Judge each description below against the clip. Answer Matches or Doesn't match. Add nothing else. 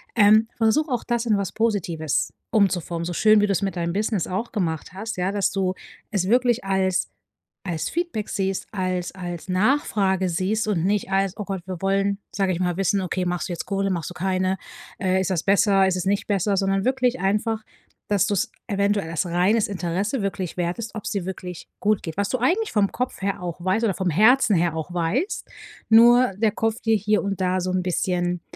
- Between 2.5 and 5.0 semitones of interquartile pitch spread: Matches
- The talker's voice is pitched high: Matches